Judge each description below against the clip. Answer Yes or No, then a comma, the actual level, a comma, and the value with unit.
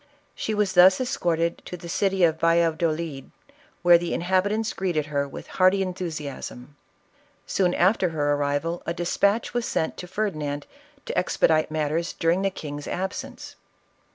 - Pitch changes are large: No, average, 3.4 semitones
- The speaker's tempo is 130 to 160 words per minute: Yes, average, 150 wpm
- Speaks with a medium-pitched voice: Yes, medium, 170 Hz